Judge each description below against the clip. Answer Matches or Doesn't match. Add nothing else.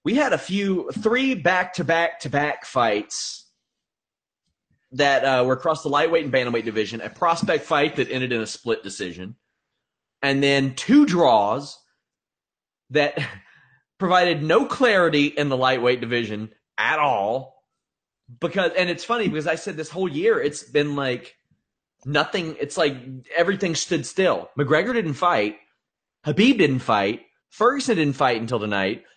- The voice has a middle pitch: Matches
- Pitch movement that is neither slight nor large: Doesn't match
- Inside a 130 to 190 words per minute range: Matches